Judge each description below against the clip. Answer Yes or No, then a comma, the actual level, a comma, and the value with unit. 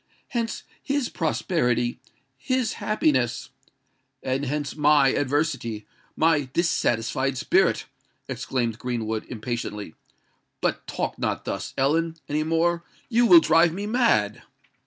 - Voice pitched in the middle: Yes, medium, 145 Hz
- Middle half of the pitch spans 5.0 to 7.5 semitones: Yes, wide, 5.5 semitones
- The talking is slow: Yes, slow, 100 wpm